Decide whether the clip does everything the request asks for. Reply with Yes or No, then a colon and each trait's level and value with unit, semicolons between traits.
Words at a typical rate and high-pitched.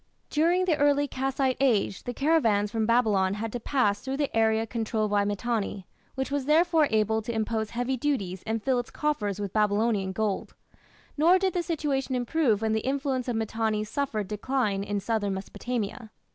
Yes: average, 175 wpm; high, 230 Hz